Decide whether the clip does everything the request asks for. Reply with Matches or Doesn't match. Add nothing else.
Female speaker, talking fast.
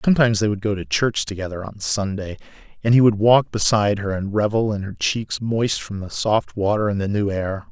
Doesn't match